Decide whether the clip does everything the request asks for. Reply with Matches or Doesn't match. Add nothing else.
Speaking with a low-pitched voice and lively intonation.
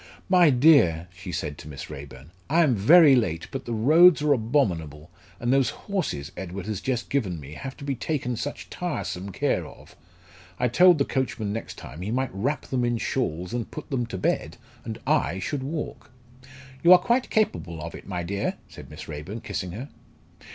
Matches